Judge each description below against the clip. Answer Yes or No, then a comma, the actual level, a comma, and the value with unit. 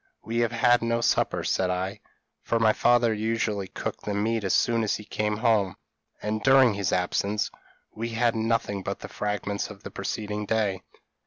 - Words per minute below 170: No, average, 180 wpm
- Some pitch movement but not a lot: No, narrow, 2.1 semitones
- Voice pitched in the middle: No, low, 110 Hz